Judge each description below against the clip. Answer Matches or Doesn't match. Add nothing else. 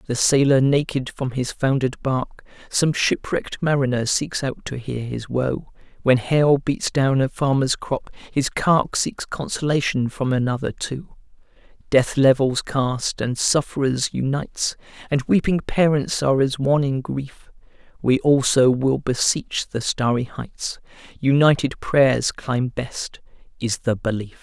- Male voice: Matches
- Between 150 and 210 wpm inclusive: Doesn't match